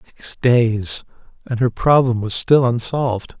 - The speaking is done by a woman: No, male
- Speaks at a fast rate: No, average, 140 wpm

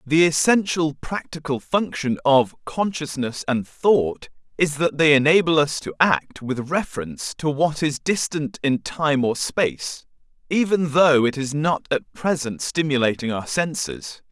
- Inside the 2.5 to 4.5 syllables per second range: Yes, 4.2 syllables/s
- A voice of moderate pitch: Yes, medium, 150 Hz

